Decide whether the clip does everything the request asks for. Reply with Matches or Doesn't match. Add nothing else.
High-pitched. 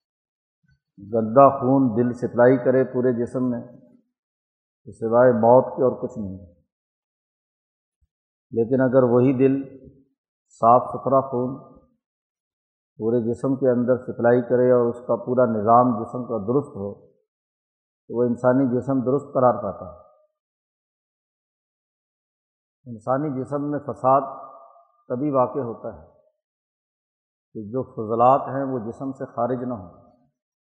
Doesn't match